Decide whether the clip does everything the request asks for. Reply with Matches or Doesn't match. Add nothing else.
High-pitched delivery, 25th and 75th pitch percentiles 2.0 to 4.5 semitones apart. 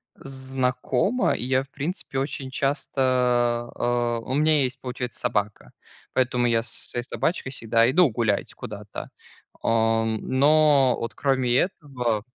Doesn't match